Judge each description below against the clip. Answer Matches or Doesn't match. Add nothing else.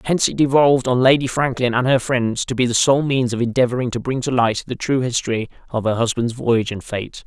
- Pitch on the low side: Matches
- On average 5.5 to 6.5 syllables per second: Matches